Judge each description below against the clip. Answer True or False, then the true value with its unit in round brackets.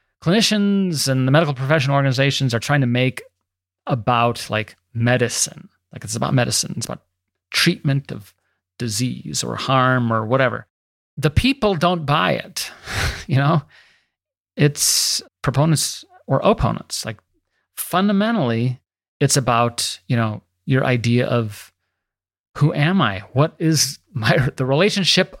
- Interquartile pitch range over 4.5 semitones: True (5.0 semitones)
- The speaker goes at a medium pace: False (130 wpm)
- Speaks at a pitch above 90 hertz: True (135 Hz)